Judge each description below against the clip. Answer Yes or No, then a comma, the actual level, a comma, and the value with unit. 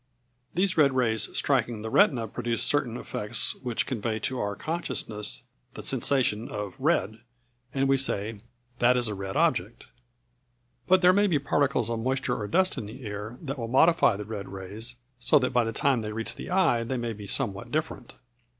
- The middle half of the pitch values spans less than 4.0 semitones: No, average, 4.3 semitones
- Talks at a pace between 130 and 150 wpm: No, average, 185 wpm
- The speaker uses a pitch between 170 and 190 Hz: No, low, 120 Hz